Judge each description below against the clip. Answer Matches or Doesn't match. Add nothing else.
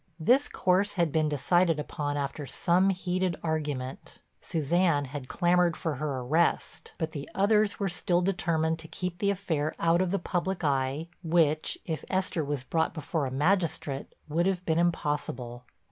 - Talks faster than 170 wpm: Doesn't match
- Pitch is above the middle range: Doesn't match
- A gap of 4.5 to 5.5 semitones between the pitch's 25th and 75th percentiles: Doesn't match